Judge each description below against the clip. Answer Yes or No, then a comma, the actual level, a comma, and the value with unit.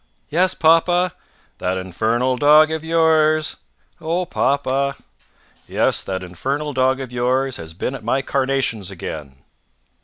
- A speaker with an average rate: No, slow, 130 wpm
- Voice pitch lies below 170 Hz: Yes, low, 135 Hz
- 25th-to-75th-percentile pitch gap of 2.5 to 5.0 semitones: No, wide, 5.5 semitones